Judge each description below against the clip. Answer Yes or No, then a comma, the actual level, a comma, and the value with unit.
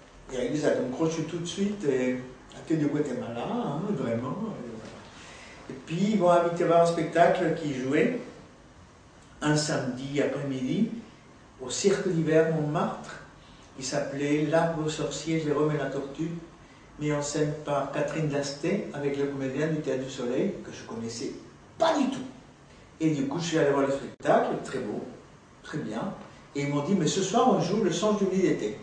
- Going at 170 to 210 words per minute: Yes, average, 180 wpm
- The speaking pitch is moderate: Yes, medium, 155 Hz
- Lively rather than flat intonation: No, average, 3.5 semitones